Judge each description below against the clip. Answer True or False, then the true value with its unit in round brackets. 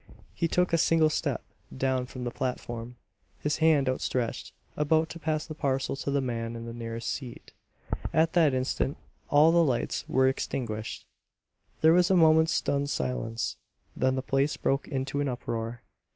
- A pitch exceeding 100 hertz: True (135 Hz)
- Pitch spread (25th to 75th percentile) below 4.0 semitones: False (4.4 semitones)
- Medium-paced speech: True (165 wpm)